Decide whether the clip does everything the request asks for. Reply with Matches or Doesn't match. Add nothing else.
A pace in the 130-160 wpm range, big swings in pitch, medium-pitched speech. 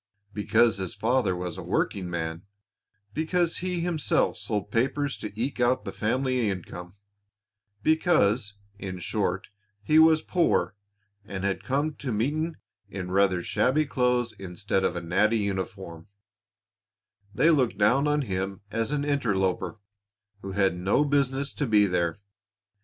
Doesn't match